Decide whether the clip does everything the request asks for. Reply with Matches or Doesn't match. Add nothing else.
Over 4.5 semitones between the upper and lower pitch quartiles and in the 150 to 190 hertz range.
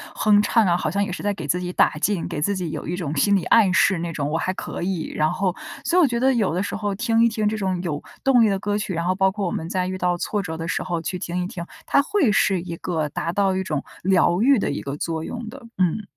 Doesn't match